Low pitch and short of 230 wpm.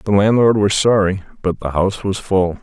Yes: low, 100 Hz; fast, 205 wpm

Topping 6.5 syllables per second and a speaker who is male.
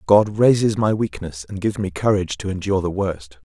No: 5.8 syllables/s; male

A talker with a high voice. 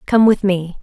Yes: high, 195 Hz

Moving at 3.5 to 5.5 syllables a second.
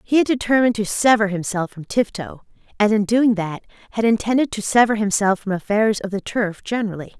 No: 5.8 syllables/s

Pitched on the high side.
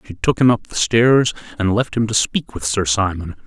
No: low, 105 Hz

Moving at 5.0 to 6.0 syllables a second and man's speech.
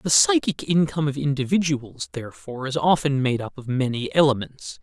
Yes: 5.5 syllables/s; male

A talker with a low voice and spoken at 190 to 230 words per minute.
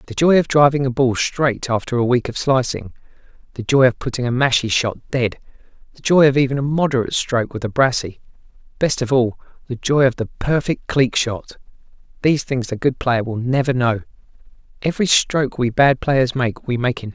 Yes: low, 130 Hz; average, 200 wpm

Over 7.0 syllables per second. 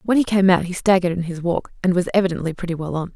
Yes: 7.2 syllables/s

